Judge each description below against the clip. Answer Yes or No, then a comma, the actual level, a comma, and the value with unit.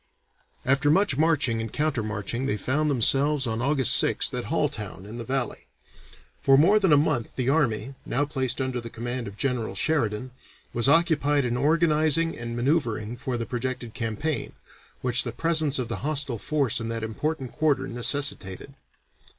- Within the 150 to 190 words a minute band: Yes, average, 165 wpm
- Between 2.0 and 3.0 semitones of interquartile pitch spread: No, average, 4.2 semitones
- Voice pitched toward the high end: No, low, 130 Hz